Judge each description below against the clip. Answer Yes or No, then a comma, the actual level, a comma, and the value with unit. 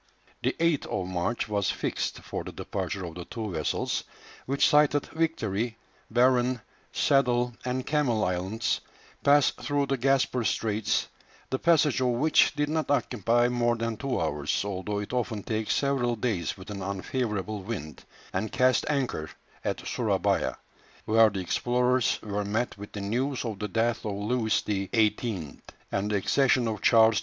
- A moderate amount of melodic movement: Yes, average, 3.9 semitones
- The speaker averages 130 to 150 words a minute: No, average, 160 wpm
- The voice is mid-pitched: No, low, 115 Hz